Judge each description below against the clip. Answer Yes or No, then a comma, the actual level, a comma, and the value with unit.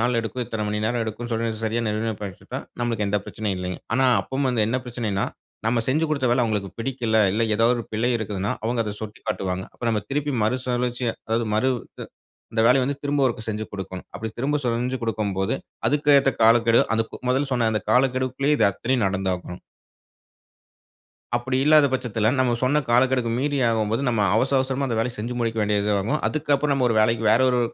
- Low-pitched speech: Yes, low, 115 Hz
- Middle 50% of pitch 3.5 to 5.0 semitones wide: No, average, 3.0 semitones